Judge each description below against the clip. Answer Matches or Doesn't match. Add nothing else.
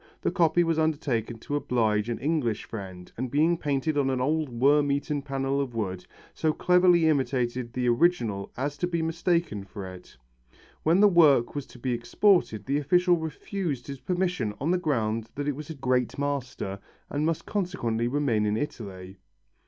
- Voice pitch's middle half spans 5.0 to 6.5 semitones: Matches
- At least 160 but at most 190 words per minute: Matches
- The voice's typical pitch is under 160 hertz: Matches